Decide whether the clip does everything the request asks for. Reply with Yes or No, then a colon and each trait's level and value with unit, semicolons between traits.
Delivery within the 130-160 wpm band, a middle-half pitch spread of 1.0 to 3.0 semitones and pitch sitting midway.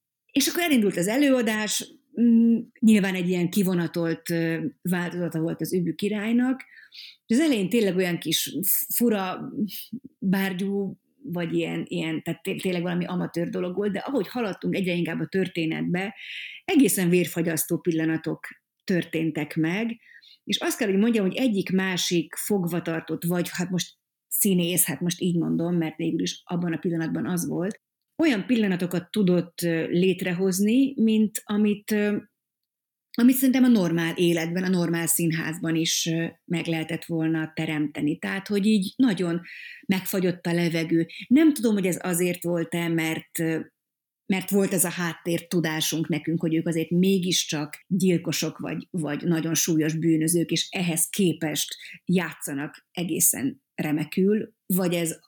No: average, 135 wpm; average, 3.9 semitones; medium, 180 Hz